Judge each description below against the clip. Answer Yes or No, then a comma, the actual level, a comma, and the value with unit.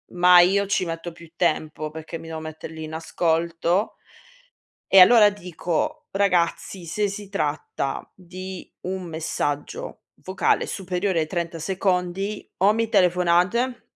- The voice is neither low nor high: Yes, medium, 180 Hz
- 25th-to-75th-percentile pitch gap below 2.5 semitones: No, average, 2.9 semitones